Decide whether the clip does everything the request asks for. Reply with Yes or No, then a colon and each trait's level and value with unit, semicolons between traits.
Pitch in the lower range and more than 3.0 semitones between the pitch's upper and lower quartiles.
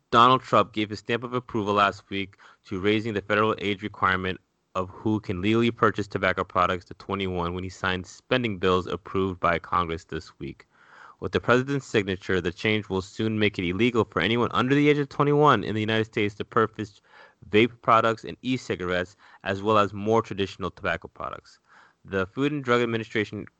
Yes: low, 105 Hz; average, 3.6 semitones